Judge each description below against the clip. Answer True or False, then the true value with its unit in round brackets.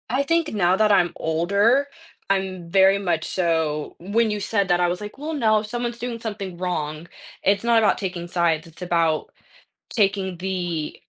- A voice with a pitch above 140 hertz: True (190 Hz)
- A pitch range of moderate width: True (3.9 semitones)